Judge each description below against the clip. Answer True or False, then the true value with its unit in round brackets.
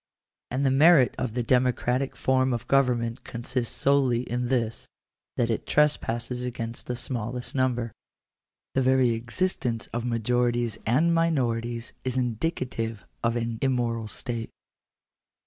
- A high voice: False (125 Hz)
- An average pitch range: False (1.9 semitones)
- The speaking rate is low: True (130 wpm)